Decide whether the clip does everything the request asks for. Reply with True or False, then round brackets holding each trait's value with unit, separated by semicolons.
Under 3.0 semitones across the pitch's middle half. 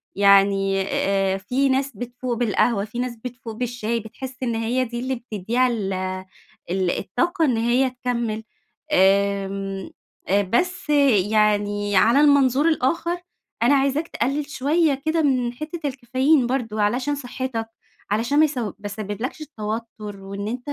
False (4.4 semitones)